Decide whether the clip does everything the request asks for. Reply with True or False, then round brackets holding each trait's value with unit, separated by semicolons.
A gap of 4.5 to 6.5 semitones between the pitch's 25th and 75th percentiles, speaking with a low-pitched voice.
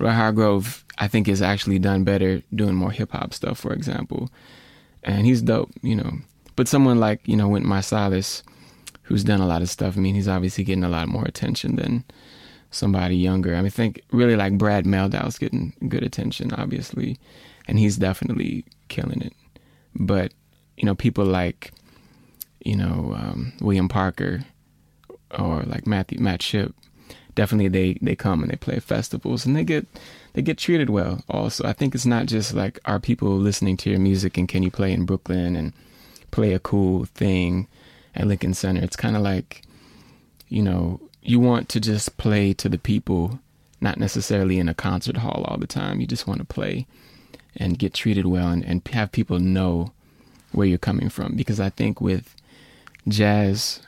False (2.6 semitones; 100 Hz)